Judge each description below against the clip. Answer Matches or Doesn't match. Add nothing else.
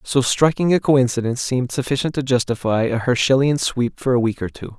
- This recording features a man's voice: Matches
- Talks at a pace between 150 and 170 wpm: Doesn't match